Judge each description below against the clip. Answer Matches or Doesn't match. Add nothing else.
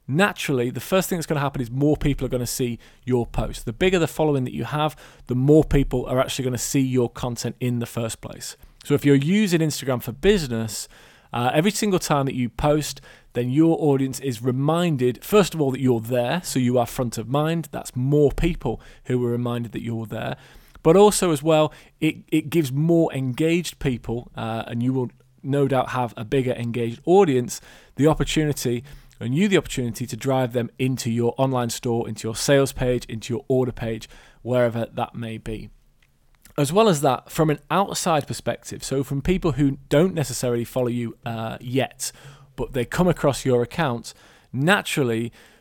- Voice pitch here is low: Matches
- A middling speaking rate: Matches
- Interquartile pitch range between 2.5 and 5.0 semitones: Matches